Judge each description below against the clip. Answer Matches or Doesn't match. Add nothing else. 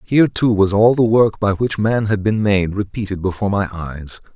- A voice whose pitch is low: Matches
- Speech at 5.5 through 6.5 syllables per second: Doesn't match